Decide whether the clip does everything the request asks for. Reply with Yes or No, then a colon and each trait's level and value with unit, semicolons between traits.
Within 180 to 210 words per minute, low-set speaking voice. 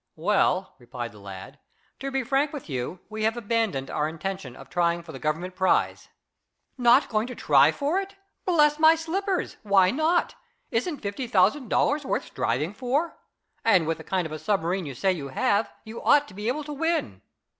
No: average, 190 wpm; high, 210 Hz